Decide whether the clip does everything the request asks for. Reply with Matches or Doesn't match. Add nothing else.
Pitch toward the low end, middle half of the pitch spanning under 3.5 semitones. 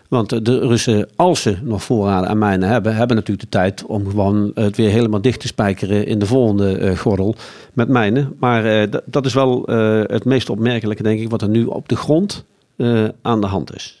Matches